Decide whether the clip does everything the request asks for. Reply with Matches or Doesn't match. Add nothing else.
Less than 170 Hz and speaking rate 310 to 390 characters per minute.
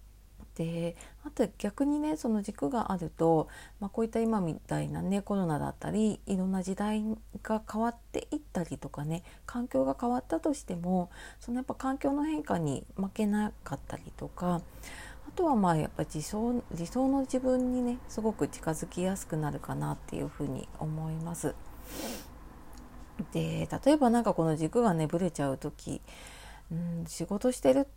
Doesn't match